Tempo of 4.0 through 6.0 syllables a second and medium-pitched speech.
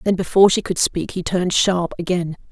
Yes: 5.8 syllables/s; medium, 180 Hz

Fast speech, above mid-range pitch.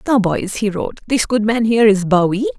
Yes: fast, 230 wpm; high, 215 Hz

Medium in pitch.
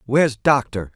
No: low, 120 Hz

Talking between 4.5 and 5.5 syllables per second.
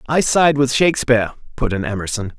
No: 6.0 syllables/s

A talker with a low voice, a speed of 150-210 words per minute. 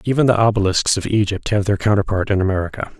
Yes: low, 100 Hz; average, 200 wpm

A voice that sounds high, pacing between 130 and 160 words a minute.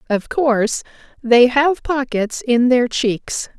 Yes: very high, 250 Hz; slow, 135 wpm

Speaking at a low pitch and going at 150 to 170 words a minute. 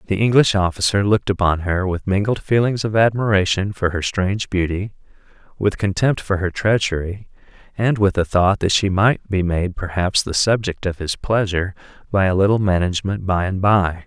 No: very low, 95 Hz; average, 180 wpm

